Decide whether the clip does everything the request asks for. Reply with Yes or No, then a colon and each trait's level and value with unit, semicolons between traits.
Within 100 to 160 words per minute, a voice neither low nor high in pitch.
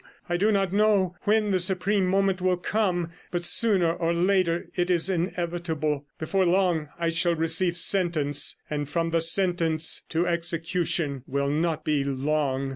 Yes: average, 155 wpm; medium, 170 Hz